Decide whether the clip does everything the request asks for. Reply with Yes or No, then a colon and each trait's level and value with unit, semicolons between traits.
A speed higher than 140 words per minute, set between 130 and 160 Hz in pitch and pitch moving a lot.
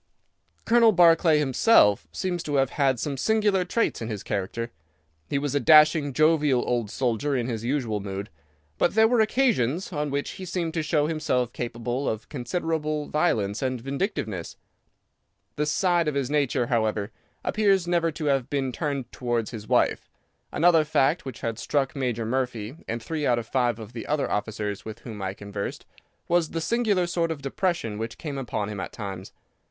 Yes: average, 180 wpm; low, 135 Hz; wide, 5.9 semitones